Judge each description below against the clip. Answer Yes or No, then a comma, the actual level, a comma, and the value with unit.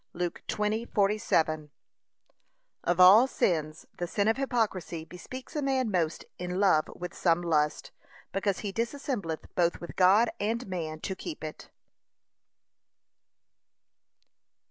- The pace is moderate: No, slow, 120 wpm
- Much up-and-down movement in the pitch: No, average, 4.7 semitones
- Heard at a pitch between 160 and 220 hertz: Yes, medium, 185 Hz